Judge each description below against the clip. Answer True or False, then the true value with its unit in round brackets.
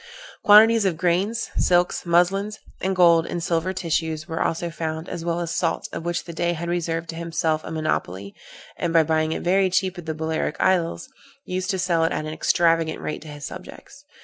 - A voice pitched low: False (170 Hz)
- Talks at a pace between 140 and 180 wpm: False (200 wpm)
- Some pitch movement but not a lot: False (2.2 semitones)